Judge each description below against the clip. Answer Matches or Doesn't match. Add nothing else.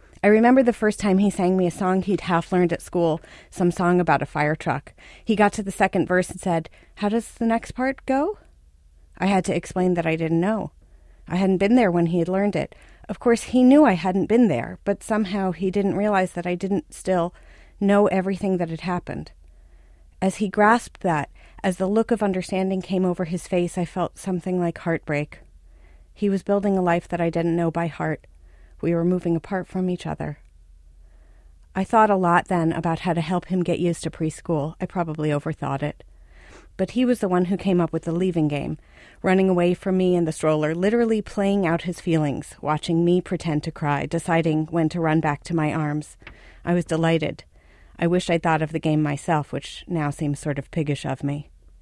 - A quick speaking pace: Matches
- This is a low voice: Doesn't match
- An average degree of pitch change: Matches